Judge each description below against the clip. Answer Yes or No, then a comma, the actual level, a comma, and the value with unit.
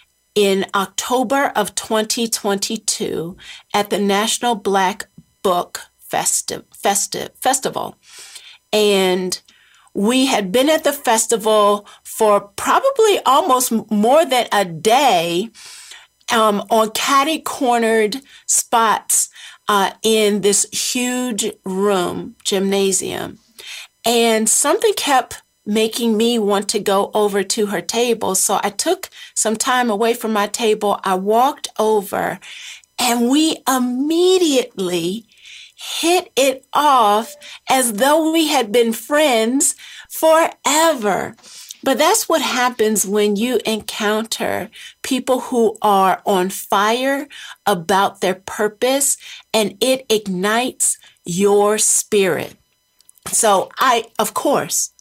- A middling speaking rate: No, slow, 105 wpm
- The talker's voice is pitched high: Yes, high, 225 Hz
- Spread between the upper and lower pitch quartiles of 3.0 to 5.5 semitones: Yes, average, 4.1 semitones